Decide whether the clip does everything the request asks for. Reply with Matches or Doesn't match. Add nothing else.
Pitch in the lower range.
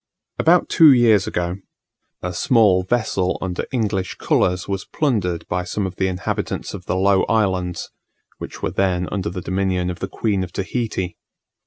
Matches